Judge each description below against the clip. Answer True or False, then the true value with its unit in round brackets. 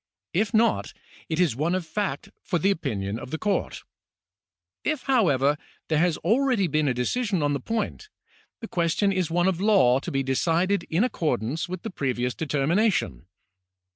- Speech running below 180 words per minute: True (170 wpm)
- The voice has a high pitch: False (170 Hz)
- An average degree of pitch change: False (6.1 semitones)